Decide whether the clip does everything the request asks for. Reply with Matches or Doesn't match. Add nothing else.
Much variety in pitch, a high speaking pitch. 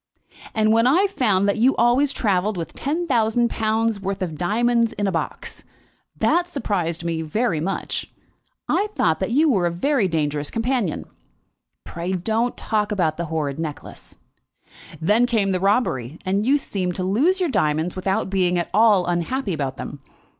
Matches